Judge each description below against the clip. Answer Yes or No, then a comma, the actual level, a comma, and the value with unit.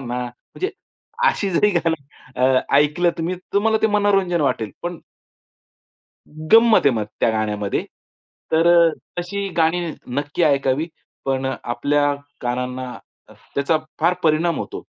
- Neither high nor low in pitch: Yes, medium, 155 Hz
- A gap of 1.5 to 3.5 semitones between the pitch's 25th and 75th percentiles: No, wide, 5.5 semitones